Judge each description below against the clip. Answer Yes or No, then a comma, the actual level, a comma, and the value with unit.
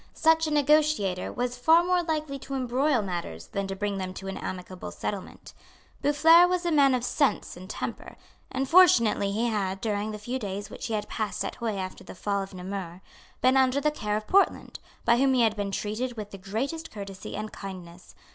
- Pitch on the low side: No, high, 220 Hz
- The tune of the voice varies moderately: No, wide, 6.0 semitones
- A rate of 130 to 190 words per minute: No, fast, 205 wpm